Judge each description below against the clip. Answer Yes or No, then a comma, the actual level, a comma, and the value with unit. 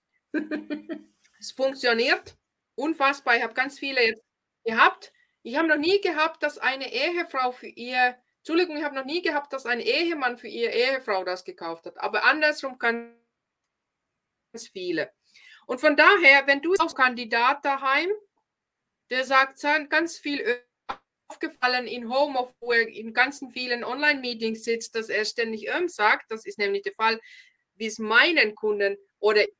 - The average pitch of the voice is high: Yes, very high, 270 Hz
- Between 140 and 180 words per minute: Yes, average, 155 wpm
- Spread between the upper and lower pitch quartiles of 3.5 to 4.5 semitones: No, average, 5.0 semitones